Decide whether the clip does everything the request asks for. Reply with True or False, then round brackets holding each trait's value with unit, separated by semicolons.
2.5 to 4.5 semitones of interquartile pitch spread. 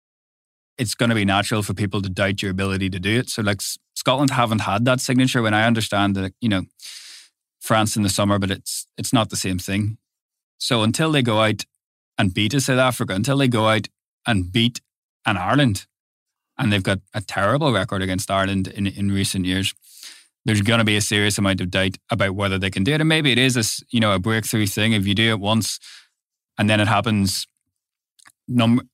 True (3.2 semitones)